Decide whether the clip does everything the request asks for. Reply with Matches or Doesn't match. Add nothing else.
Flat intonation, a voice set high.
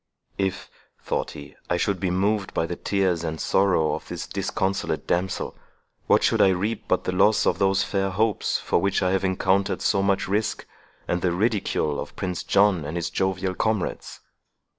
Doesn't match